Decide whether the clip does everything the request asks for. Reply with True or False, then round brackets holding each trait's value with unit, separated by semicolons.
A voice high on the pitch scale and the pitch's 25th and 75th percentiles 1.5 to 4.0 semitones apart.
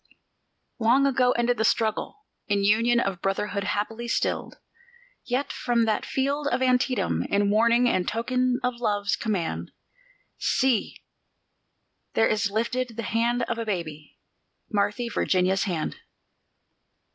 True (230 Hz; 3.3 semitones)